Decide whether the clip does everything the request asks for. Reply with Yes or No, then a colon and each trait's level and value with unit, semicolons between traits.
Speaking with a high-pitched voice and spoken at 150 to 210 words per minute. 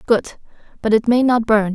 Yes: high, 225 Hz; fast, 205 wpm